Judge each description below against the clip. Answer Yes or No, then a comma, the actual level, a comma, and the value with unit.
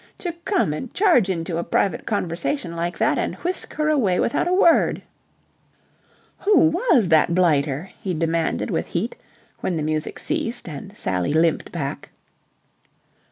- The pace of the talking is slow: No, average, 150 wpm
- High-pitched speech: No, medium, 180 Hz